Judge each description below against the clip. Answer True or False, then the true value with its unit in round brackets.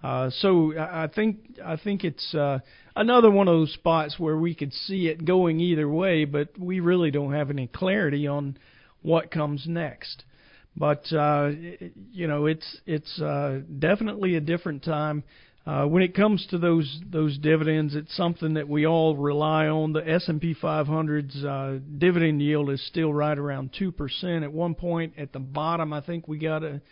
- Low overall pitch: False (155 Hz)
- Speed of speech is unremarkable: True (185 wpm)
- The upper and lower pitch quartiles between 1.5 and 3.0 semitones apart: True (2.6 semitones)